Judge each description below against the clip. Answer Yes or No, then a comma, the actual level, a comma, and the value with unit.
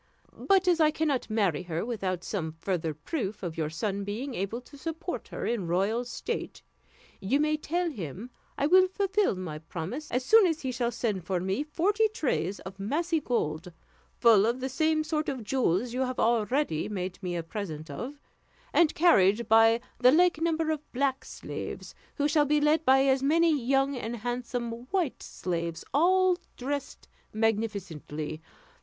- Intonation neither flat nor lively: No, wide, 7.8 semitones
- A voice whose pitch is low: No, high, 245 Hz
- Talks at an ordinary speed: Yes, average, 170 wpm